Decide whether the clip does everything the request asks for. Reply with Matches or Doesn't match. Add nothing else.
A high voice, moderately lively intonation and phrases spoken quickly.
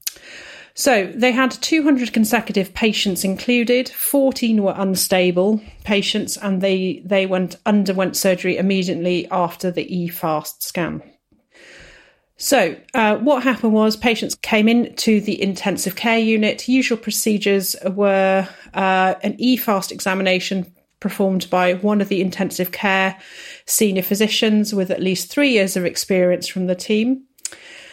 Doesn't match